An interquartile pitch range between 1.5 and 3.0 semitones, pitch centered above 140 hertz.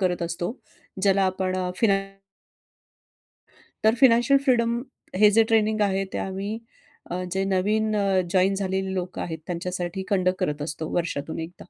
Yes: average, 2.7 semitones; high, 190 Hz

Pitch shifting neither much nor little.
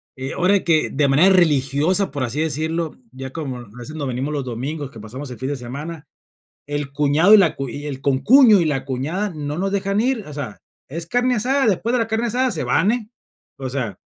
No: wide, 6.4 semitones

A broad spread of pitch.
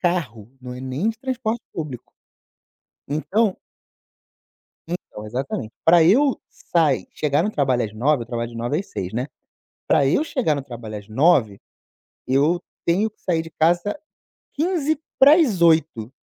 Yes: wide, 8.6 semitones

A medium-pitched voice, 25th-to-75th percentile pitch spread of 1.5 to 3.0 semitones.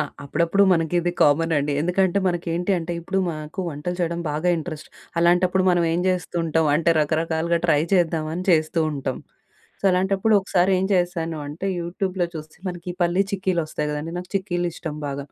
Yes: medium, 170 Hz; narrow, 2.4 semitones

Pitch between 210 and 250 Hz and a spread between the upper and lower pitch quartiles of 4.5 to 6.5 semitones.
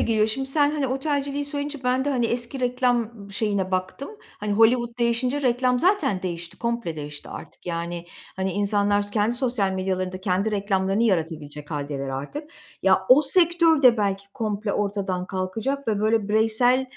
Yes: high, 215 Hz; average, 5.1 semitones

